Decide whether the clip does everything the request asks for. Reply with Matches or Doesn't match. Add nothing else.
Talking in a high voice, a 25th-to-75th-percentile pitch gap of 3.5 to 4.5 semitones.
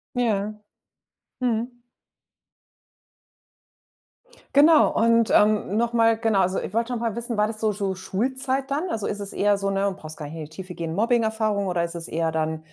Matches